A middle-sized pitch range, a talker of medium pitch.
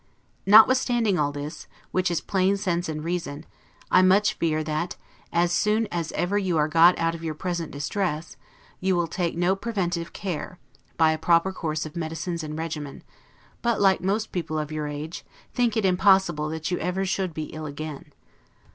Yes: average, 3.4 semitones; medium, 170 Hz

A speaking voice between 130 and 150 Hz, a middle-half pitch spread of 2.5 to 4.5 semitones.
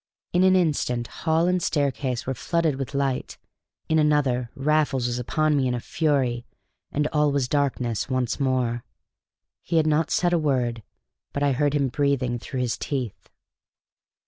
Yes: medium, 140 Hz; average, 3.4 semitones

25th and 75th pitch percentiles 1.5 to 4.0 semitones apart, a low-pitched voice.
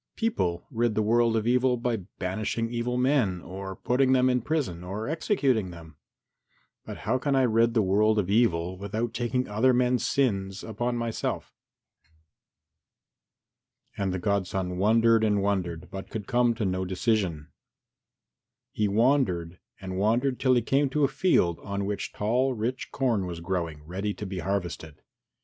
No: average, 4.7 semitones; low, 110 Hz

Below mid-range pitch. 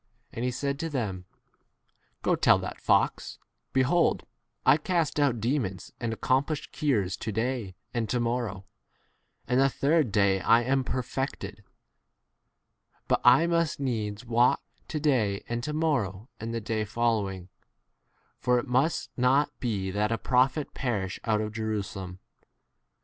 Yes: low, 120 Hz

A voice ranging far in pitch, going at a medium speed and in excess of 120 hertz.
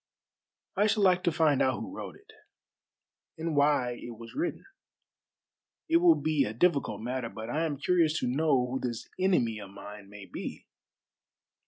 Yes: wide, 6.3 semitones; average, 170 wpm; medium, 140 Hz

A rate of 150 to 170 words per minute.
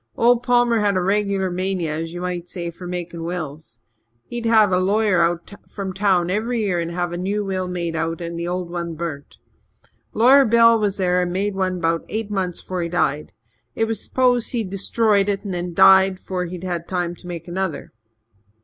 No: average, 195 wpm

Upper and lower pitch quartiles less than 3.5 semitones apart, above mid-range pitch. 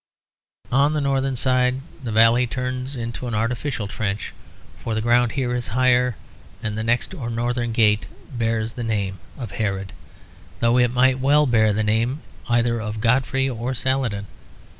No: narrow, 2.4 semitones; low, 120 Hz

